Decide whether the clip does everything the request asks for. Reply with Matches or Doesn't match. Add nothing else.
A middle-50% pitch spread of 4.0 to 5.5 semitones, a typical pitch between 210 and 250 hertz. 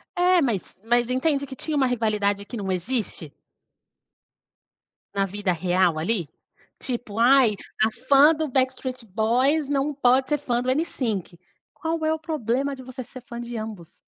Matches